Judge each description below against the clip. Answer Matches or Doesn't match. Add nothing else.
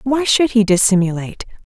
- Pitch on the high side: Matches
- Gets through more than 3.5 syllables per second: Matches